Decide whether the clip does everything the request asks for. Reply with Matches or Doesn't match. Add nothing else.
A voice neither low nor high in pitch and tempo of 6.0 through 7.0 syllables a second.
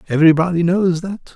Matches